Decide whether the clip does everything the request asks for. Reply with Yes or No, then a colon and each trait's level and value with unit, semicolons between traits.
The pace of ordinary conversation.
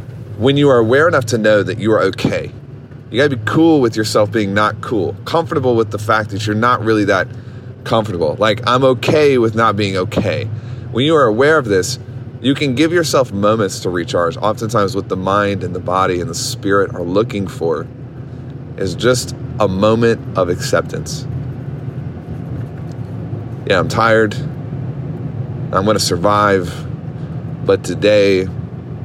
Yes: average, 160 wpm